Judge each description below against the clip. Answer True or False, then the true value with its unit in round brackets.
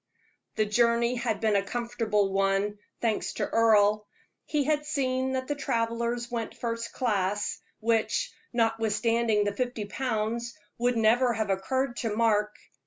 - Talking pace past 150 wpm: False (140 wpm)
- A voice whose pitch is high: True (230 Hz)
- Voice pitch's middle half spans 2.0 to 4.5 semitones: True (2.4 semitones)